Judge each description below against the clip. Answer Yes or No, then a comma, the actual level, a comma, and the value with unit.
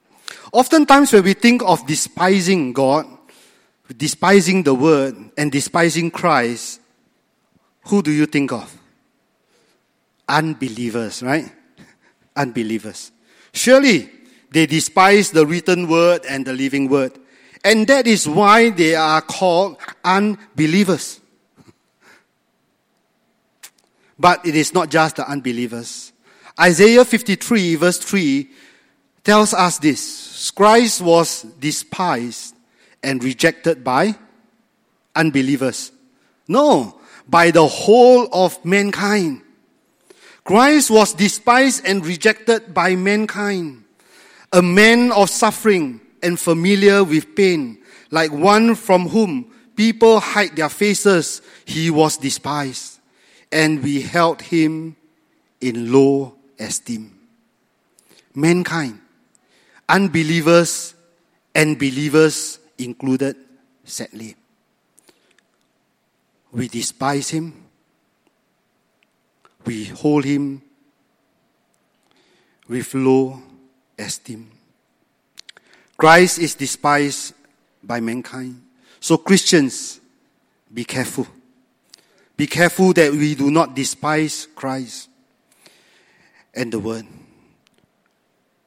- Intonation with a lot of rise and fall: Yes, wide, 6.8 semitones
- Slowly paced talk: Yes, slow, 90 wpm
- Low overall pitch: No, medium, 165 Hz